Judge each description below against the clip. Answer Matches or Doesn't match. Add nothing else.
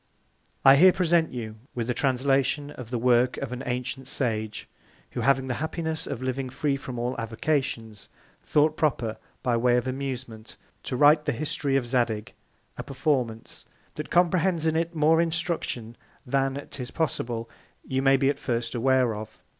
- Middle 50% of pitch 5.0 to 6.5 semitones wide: Doesn't match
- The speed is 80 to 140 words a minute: Doesn't match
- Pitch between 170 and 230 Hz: Doesn't match